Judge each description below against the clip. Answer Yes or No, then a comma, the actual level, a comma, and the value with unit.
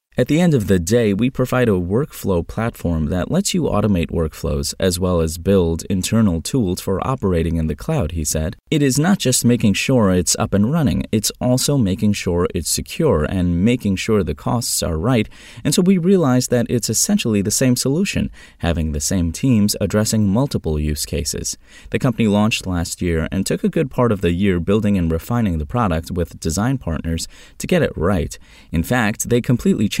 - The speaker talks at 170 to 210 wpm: Yes, average, 200 wpm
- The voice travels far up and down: Yes, wide, 6.5 semitones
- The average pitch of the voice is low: Yes, low, 100 Hz